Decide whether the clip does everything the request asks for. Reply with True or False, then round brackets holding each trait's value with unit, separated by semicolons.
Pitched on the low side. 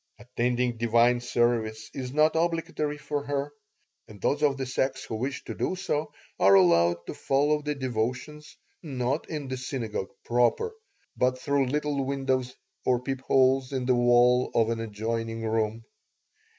True (125 Hz)